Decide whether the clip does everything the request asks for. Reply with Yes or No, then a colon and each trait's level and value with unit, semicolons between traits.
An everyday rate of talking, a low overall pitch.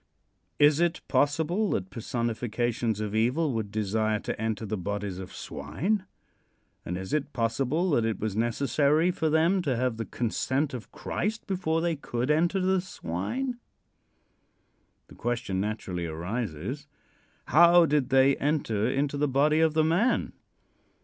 Yes: average, 145 wpm; low, 130 Hz